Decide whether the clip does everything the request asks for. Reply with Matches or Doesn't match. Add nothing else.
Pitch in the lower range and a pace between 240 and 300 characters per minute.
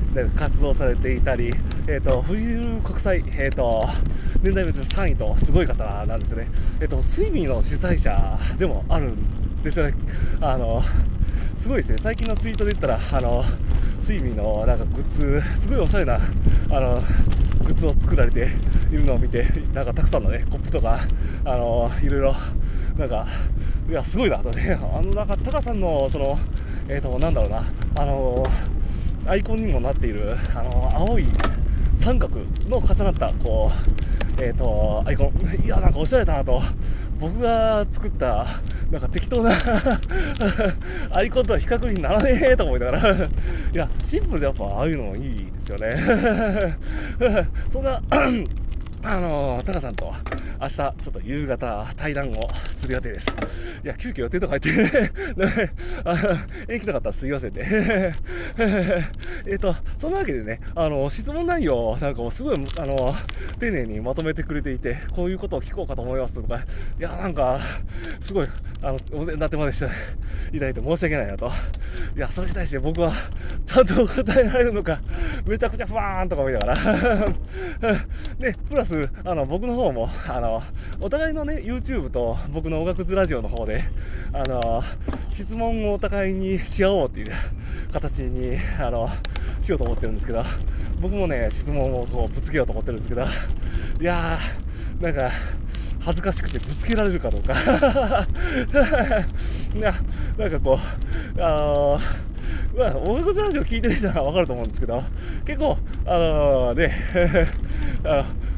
Doesn't match